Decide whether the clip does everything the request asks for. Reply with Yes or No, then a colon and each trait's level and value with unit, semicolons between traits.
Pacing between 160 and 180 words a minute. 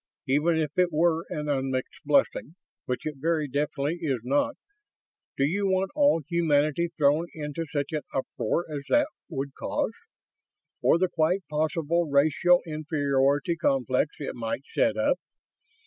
No: average, 145 wpm